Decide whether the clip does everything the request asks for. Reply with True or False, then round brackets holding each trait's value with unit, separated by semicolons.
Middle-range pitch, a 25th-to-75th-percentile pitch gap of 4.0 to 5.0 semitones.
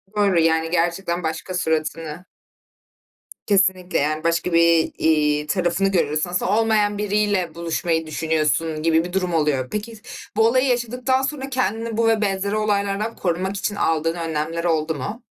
True (180 Hz; 4.3 semitones)